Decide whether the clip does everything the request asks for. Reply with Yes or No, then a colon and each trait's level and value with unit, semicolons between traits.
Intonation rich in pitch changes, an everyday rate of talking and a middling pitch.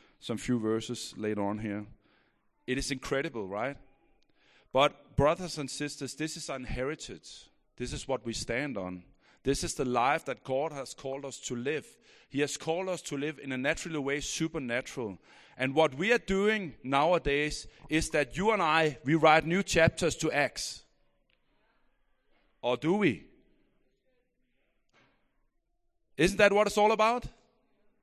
Yes: wide, 5.7 semitones; average, 150 wpm; medium, 150 Hz